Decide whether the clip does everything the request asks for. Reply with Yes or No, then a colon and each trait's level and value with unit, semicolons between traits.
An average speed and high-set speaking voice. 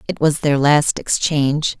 No: average, 165 wpm; medium, 145 Hz